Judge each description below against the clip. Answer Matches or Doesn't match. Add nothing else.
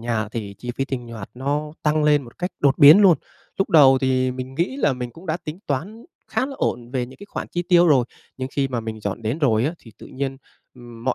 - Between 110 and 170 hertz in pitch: Matches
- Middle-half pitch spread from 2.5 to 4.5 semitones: Matches